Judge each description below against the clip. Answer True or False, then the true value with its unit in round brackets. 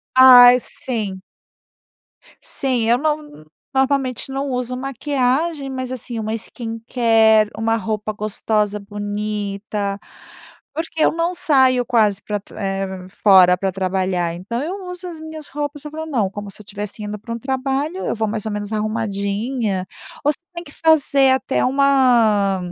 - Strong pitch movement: False (4.7 semitones)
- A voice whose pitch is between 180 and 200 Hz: False (230 Hz)